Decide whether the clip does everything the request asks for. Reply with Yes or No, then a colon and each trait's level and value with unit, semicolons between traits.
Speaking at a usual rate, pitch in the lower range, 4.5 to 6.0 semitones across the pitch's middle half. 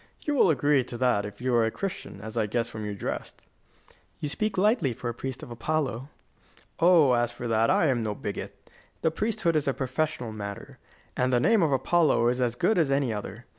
No: fast, 215 wpm; low, 125 Hz; average, 5.2 semitones